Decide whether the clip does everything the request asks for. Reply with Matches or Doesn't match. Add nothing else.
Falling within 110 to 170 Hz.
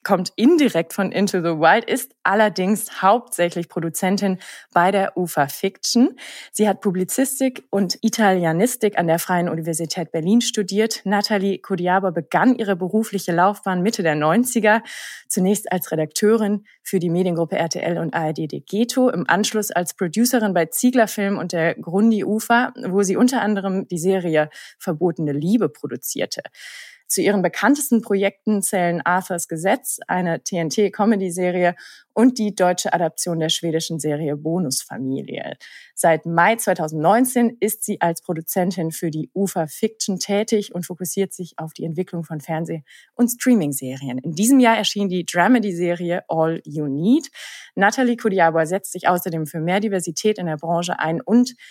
Doesn't match